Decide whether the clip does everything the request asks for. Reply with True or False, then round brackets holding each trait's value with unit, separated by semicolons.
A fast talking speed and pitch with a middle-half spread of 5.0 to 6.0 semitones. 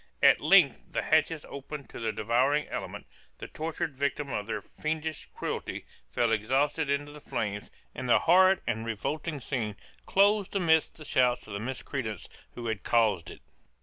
False (165 wpm; 5.6 semitones)